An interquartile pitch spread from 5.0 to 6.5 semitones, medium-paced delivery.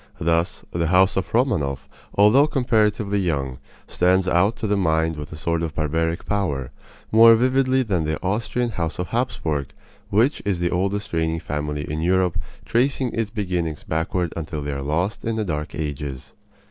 Yes: average, 5.3 semitones; average, 170 wpm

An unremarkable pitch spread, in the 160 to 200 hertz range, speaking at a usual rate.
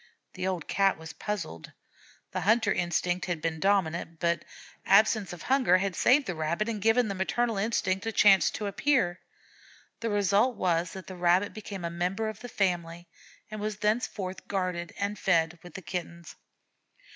Yes: average, 3.5 semitones; high, 190 Hz; average, 170 wpm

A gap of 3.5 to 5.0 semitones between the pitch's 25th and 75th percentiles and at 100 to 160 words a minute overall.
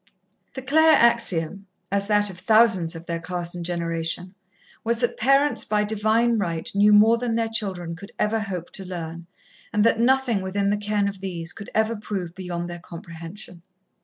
No: average, 4.3 semitones; average, 180 wpm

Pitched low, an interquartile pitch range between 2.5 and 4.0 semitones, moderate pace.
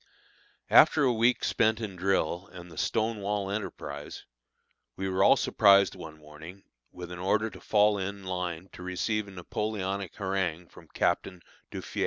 Yes: very low, 95 Hz; average, 2.8 semitones; average, 160 wpm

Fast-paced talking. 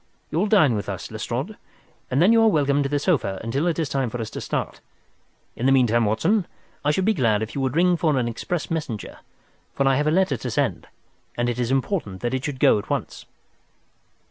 Yes: fast, 225 wpm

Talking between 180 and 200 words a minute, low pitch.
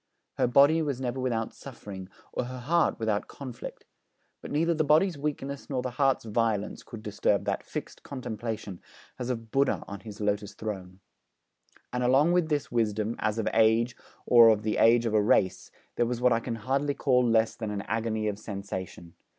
Yes: average, 185 wpm; low, 115 Hz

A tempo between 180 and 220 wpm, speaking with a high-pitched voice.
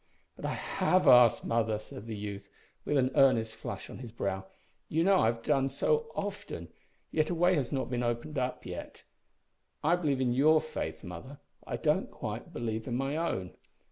No: average, 190 wpm; low, 130 Hz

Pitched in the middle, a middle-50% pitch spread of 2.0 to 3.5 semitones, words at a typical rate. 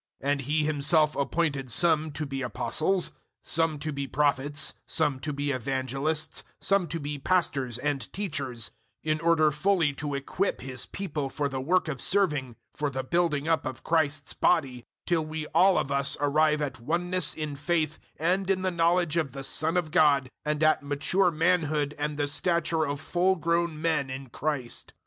Yes: medium, 150 Hz; average, 3.1 semitones; average, 180 wpm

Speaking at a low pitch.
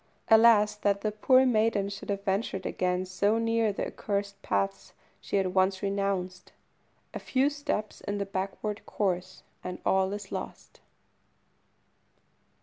No: high, 200 Hz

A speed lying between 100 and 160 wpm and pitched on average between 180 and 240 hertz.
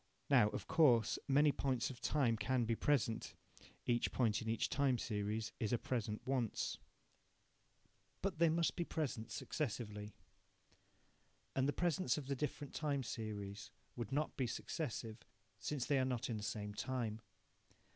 No: average, 155 wpm; low, 125 Hz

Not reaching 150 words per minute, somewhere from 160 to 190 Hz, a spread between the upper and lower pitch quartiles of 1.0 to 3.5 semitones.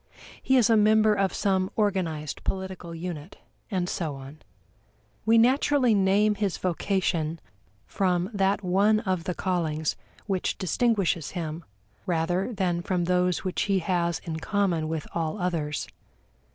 Yes: average, 140 wpm; medium, 185 Hz; average, 3.2 semitones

